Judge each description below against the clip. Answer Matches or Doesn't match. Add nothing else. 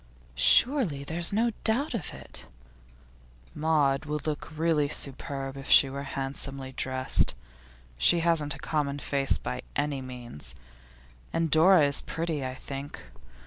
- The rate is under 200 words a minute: Matches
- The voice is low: Doesn't match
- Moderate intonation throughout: Matches